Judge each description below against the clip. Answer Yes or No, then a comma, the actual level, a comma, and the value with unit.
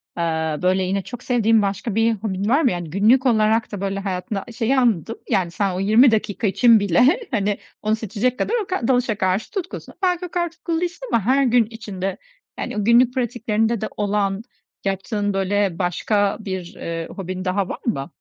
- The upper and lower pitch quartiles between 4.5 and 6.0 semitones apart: No, average, 3.8 semitones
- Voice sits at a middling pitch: No, high, 210 Hz